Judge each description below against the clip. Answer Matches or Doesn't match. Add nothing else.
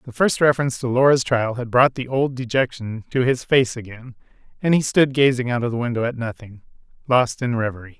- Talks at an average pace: Doesn't match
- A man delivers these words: Matches